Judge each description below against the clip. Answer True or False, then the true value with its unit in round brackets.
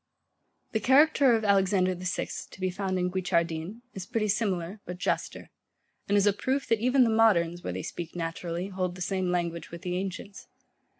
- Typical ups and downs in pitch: True (3.2 semitones)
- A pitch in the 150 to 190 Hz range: True (185 Hz)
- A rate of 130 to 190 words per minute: False (205 wpm)